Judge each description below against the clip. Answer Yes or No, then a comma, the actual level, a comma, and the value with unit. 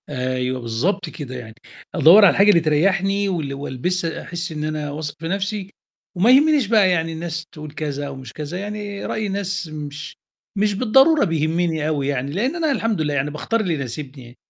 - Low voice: No, medium, 165 Hz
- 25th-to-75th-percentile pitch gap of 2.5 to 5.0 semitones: No, wide, 5.4 semitones